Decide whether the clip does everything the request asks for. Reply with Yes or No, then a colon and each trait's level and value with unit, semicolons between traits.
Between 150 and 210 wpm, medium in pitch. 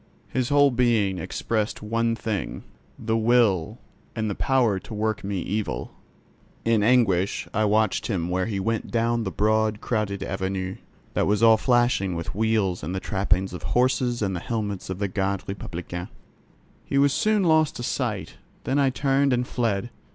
No: average, 170 wpm; low, 110 Hz